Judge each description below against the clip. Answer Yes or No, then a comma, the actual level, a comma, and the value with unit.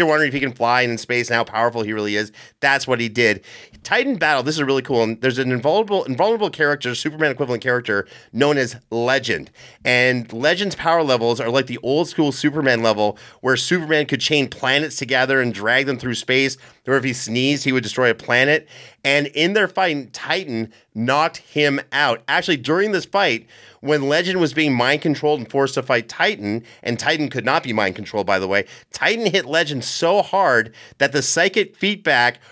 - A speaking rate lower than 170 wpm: No, average, 200 wpm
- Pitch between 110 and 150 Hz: Yes, low, 135 Hz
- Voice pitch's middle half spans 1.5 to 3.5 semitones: No, average, 4.1 semitones